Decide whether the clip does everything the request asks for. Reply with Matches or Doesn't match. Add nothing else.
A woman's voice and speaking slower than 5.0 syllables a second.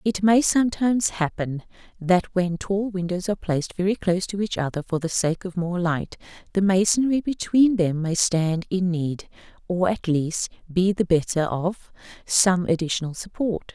Matches